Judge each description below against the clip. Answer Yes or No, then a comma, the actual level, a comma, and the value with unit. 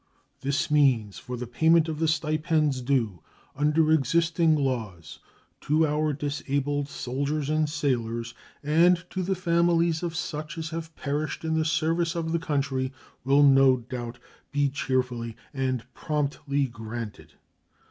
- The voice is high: No, medium, 145 Hz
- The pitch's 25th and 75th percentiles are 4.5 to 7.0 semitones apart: No, average, 3.7 semitones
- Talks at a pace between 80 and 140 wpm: Yes, slow, 135 wpm